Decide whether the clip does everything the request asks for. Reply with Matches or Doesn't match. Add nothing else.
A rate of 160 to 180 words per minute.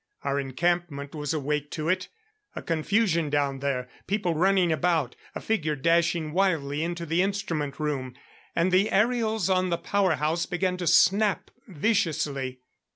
Doesn't match